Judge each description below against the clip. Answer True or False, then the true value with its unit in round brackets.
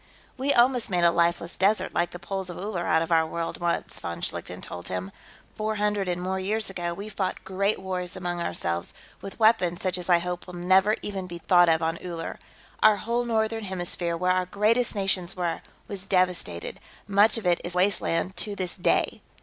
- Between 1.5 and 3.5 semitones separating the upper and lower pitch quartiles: True (2.8 semitones)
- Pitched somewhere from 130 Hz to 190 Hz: True (185 Hz)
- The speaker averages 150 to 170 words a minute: False (200 wpm)